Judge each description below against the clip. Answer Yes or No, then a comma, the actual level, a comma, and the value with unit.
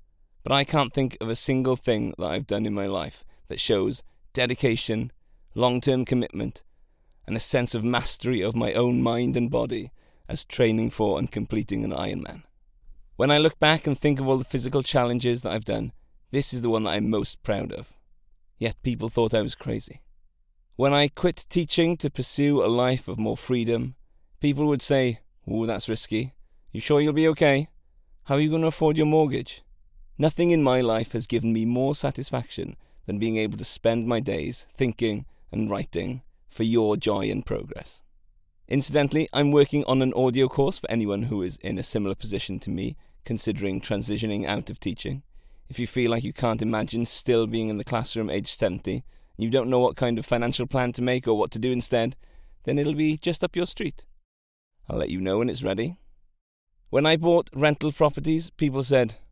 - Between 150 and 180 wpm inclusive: No, average, 195 wpm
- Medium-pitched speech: No, low, 120 Hz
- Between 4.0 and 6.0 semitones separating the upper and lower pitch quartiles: Yes, average, 4.9 semitones